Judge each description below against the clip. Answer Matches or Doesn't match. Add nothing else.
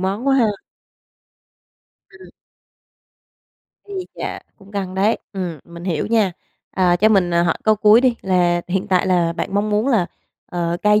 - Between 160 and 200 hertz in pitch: Matches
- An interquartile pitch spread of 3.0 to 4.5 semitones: Matches